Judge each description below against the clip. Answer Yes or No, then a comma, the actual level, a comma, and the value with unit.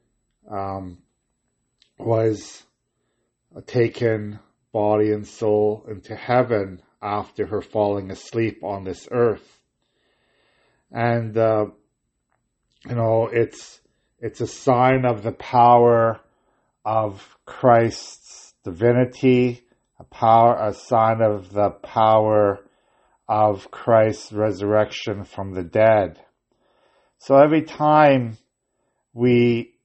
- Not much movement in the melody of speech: Yes, narrow, 2.3 semitones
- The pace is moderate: No, slow, 90 wpm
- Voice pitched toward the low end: Yes, low, 110 Hz